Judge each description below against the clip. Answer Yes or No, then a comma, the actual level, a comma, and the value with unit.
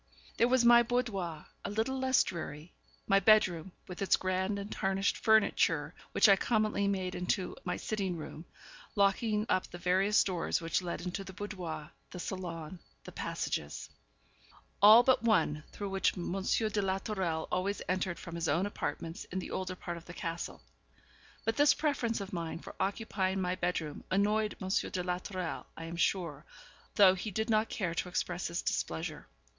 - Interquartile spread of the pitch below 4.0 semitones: Yes, average, 3.3 semitones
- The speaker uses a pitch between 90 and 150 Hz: No, high, 190 Hz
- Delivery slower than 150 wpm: No, average, 175 wpm